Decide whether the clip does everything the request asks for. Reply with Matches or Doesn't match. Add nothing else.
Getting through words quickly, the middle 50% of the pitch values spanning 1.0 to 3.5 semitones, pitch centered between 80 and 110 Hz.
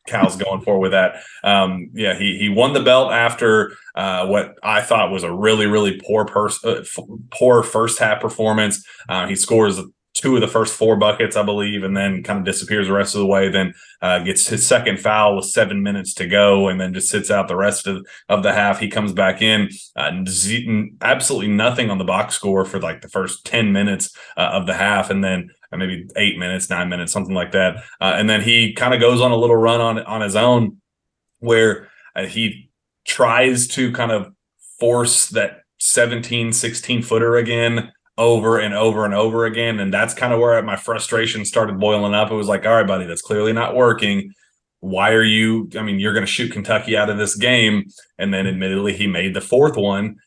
Matches